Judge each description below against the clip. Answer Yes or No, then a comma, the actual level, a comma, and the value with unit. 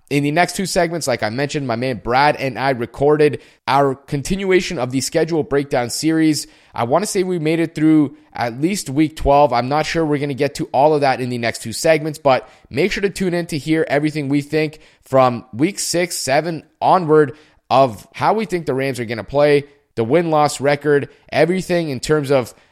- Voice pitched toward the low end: No, medium, 150 Hz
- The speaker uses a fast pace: Yes, fast, 220 wpm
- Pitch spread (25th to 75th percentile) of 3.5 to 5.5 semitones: No, average, 2.8 semitones